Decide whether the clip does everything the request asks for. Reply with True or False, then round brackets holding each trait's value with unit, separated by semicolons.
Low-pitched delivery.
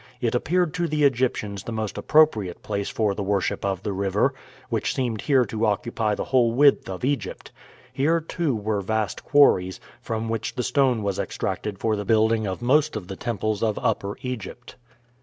True (110 Hz)